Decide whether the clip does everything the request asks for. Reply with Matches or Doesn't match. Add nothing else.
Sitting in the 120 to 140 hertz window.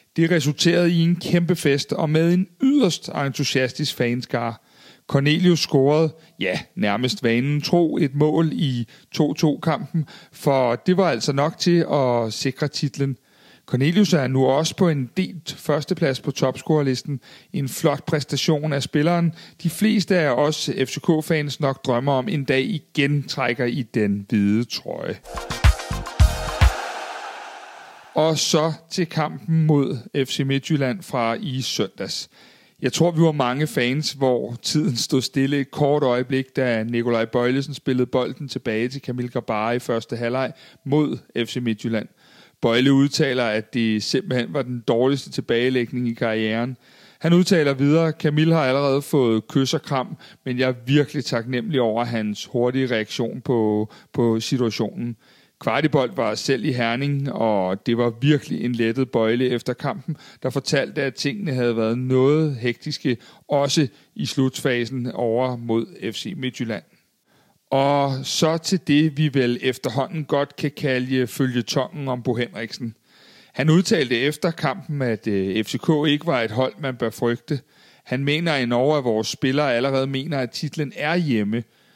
Matches